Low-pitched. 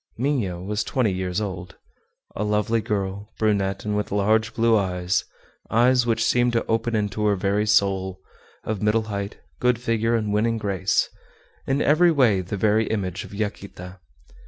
Yes: low, 105 Hz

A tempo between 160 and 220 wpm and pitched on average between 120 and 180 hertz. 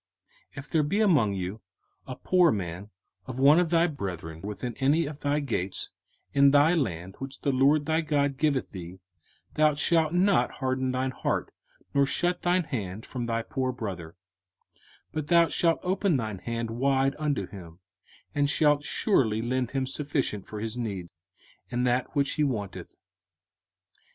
Yes: average, 165 wpm; low, 135 Hz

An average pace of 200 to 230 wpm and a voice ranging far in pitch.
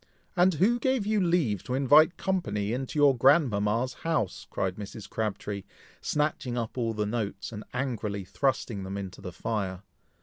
No: average, 160 wpm; wide, 6.6 semitones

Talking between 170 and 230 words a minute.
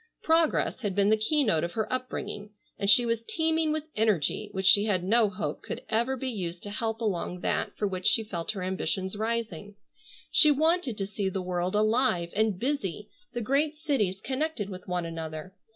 Yes: average, 190 wpm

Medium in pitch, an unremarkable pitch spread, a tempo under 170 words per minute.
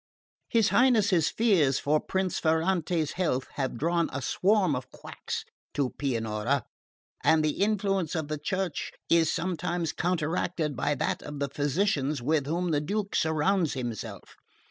Yes: medium, 160 Hz; average, 4.4 semitones; average, 145 wpm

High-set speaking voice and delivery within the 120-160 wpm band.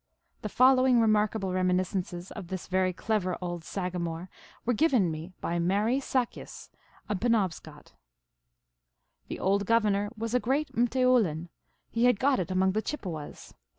Yes: high, 195 Hz; average, 150 wpm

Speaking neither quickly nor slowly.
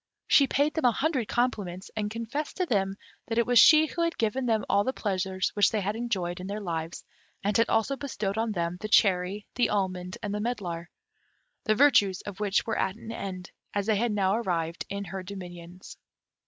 No: fast, 210 wpm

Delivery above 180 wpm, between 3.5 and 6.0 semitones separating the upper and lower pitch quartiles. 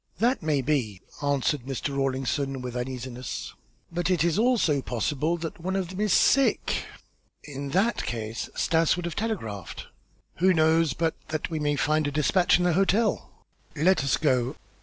No: average, 170 wpm; average, 4.8 semitones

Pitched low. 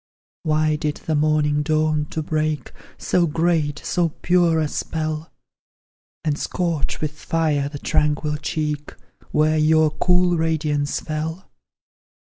No: medium, 155 Hz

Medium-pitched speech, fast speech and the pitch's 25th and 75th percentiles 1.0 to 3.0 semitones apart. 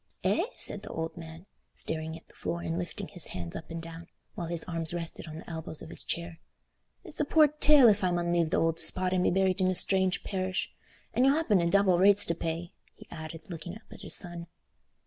Yes: medium, 170 Hz; fast, 235 wpm; narrow, 2.6 semitones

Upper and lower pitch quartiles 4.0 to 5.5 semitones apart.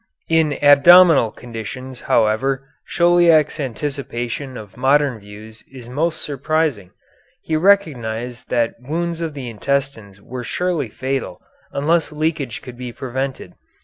Yes: average, 4.7 semitones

